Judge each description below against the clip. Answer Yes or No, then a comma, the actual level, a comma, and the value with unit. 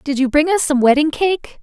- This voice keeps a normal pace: No, fast, 260 wpm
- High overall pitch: Yes, very high, 300 Hz